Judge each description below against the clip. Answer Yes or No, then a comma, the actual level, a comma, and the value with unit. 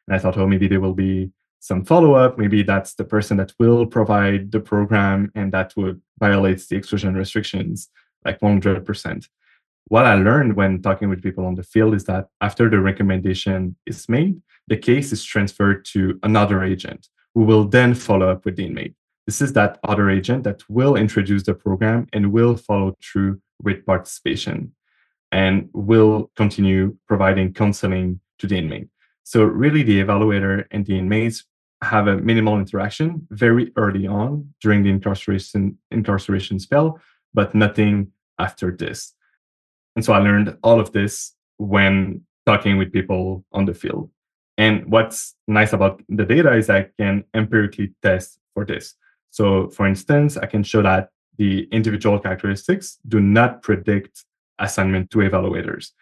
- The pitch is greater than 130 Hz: No, low, 100 Hz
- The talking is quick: No, average, 160 wpm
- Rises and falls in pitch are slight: Yes, narrow, 2.1 semitones